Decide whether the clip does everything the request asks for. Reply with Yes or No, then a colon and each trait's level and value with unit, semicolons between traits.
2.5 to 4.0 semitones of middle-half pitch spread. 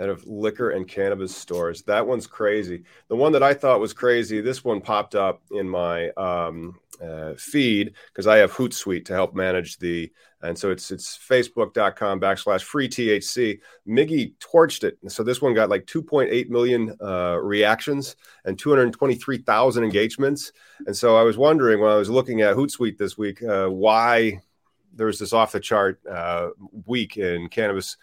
No: average, 4.5 semitones